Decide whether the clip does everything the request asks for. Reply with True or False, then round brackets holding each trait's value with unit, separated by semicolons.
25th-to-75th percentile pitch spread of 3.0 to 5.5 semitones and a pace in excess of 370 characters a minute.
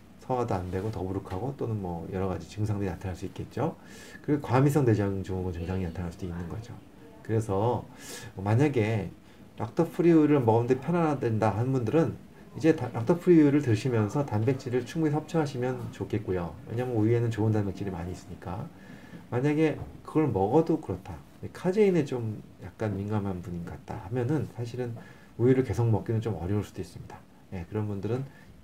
True (5.2 semitones; 380 characters per minute)